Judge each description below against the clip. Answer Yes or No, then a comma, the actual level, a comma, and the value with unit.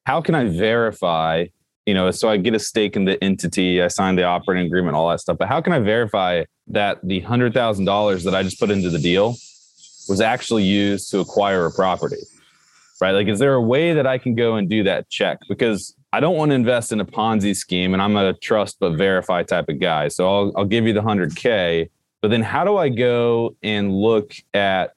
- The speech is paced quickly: Yes, fast, 225 wpm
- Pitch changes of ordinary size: Yes, average, 3.8 semitones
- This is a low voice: Yes, low, 100 Hz